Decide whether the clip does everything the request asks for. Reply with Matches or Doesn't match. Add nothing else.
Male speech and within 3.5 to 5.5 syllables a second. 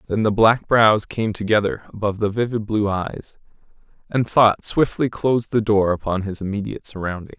Matches